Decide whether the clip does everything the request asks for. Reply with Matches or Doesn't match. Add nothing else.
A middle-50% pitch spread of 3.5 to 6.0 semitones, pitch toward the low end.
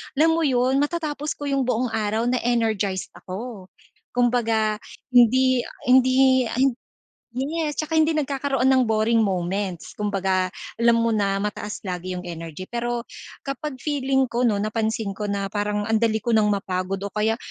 Doesn't match